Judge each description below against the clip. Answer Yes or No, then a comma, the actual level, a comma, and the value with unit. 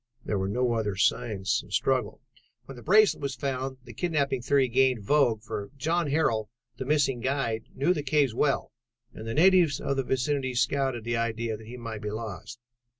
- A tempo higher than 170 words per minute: Yes, average, 190 wpm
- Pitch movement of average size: Yes, average, 3.7 semitones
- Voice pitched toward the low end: Yes, low, 130 Hz